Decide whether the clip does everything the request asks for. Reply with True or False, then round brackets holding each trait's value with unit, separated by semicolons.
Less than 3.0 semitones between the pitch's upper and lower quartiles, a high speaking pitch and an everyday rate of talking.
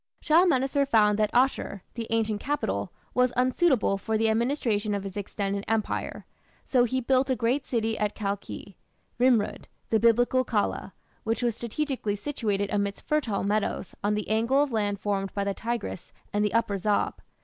False (3.7 semitones; 225 Hz; 165 wpm)